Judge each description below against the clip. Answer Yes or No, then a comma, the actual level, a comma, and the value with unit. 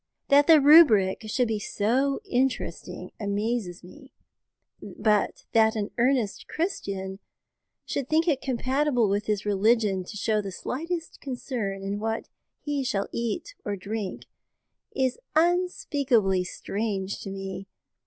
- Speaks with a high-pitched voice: Yes, high, 225 Hz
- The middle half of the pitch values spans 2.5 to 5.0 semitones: No, wide, 5.4 semitones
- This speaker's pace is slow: Yes, slow, 125 wpm